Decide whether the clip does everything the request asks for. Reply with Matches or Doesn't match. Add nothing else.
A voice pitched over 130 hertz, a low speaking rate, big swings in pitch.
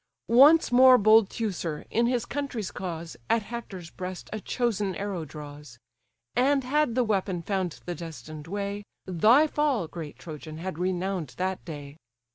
Doesn't match